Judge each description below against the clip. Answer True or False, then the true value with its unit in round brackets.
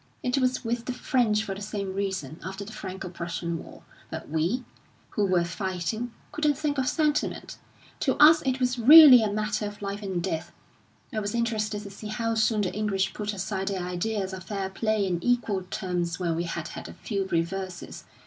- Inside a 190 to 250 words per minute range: True (195 wpm)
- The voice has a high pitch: True (205 Hz)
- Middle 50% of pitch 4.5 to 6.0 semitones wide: False (3.5 semitones)